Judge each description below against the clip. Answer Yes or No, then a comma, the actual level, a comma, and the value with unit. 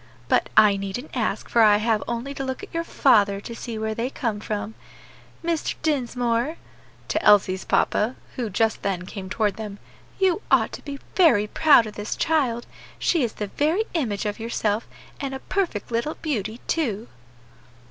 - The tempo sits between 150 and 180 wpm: Yes, average, 175 wpm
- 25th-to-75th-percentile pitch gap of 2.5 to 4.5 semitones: No, average, 5.0 semitones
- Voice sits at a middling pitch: No, high, 230 Hz